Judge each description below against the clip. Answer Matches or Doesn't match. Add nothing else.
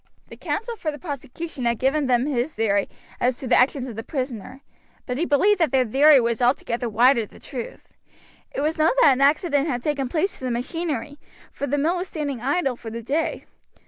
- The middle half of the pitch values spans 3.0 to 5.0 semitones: Matches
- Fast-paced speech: Matches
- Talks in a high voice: Matches